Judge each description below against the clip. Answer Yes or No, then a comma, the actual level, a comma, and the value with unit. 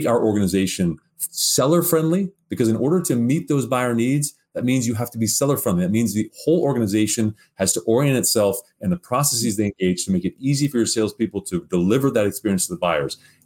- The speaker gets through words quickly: Yes, fast, 215 wpm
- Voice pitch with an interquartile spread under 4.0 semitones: No, average, 5.2 semitones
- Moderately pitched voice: No, low, 120 Hz